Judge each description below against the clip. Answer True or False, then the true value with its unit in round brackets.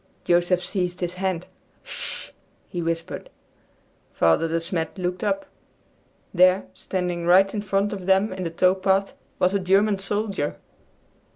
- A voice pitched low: False (185 Hz)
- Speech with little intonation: True (1.9 semitones)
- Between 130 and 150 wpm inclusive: True (145 wpm)